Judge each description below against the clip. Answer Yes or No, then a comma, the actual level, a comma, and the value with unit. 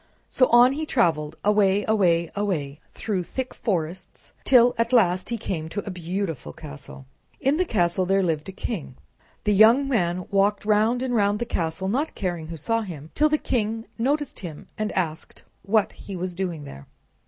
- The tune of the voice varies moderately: Yes, average, 5.0 semitones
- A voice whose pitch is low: No, high, 195 Hz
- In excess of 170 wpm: Yes, average, 180 wpm